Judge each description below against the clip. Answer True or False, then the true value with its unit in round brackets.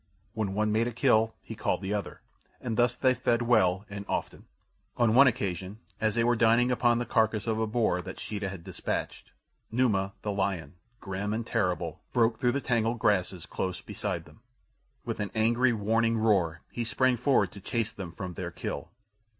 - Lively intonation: False (3.2 semitones)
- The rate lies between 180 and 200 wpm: True (190 wpm)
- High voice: False (110 Hz)